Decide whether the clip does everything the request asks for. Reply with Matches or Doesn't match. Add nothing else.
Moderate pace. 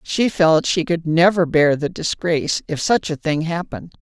Matches